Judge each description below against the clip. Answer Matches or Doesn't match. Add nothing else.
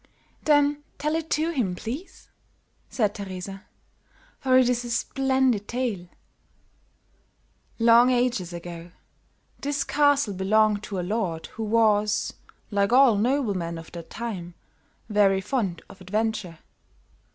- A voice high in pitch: Matches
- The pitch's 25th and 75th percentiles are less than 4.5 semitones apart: Doesn't match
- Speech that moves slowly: Matches